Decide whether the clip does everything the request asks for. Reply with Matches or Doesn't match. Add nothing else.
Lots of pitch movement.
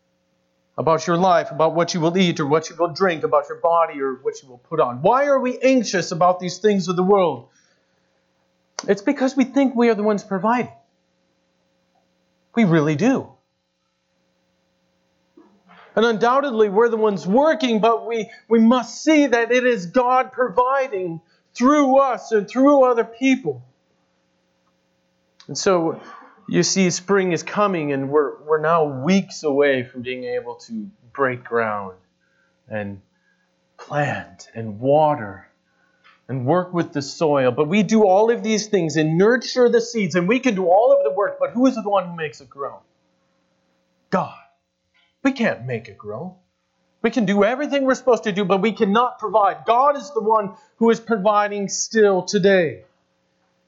Matches